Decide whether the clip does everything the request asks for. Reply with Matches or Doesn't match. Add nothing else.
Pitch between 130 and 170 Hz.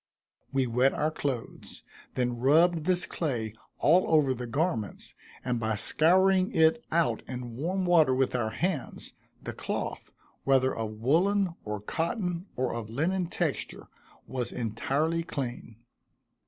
Matches